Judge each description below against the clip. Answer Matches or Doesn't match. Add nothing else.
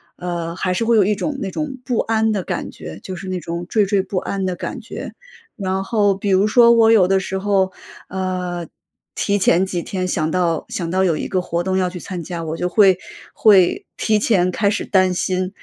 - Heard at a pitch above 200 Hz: Doesn't match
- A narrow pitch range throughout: Matches